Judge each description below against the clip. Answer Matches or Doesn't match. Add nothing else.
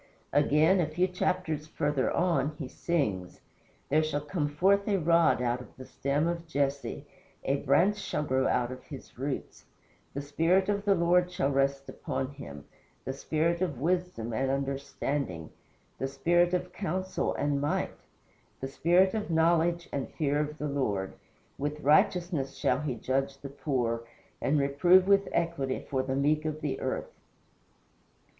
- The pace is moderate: Matches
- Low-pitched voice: Doesn't match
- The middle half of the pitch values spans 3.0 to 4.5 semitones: Matches